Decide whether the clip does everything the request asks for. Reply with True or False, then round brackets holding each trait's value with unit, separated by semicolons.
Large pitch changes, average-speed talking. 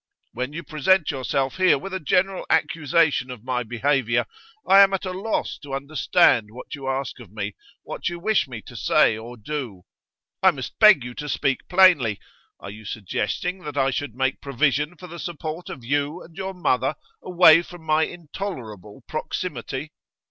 True (5.8 semitones; 175 wpm)